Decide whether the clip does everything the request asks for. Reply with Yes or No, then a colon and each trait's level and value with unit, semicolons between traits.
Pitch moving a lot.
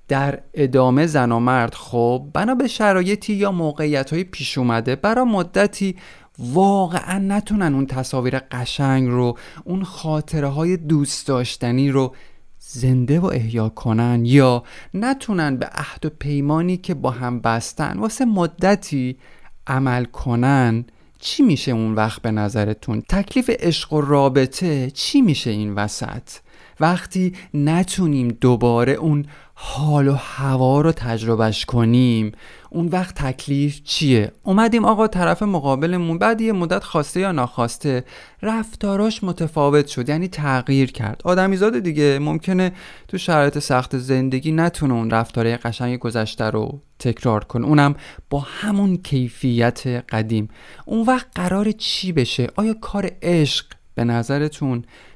Yes: wide, 6.5 semitones